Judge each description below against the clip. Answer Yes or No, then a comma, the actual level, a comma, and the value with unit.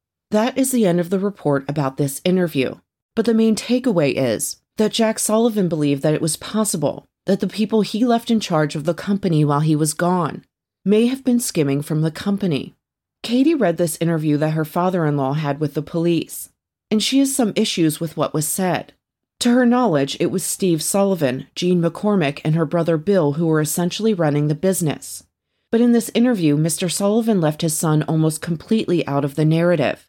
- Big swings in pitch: Yes, wide, 5.7 semitones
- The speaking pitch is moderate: Yes, medium, 170 Hz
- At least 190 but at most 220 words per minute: Yes, average, 200 wpm